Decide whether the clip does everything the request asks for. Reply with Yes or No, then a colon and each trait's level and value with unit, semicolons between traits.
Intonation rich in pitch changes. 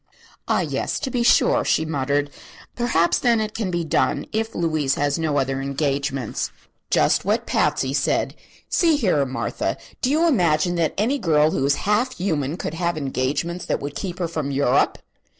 Yes: wide, 6.2 semitones